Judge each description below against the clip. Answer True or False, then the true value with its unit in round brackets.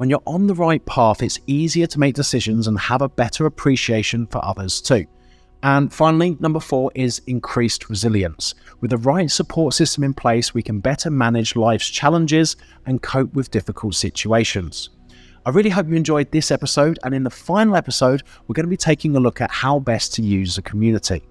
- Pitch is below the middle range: True (130 Hz)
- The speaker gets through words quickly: False (195 wpm)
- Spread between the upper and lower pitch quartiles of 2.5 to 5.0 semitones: False (5.4 semitones)